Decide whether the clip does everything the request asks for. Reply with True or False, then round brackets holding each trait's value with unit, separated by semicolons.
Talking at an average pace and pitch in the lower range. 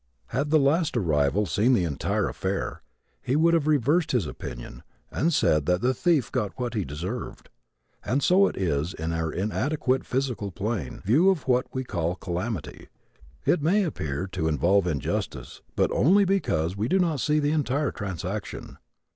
True (175 wpm; 120 Hz)